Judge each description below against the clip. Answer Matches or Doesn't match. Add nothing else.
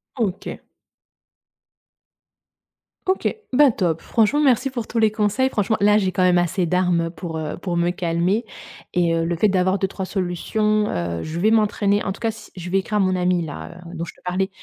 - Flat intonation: Doesn't match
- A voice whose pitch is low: Doesn't match